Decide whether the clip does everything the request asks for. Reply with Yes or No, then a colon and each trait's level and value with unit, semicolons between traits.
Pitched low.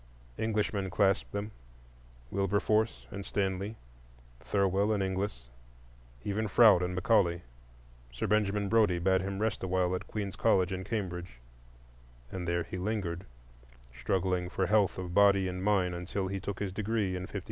Yes: very low, 95 Hz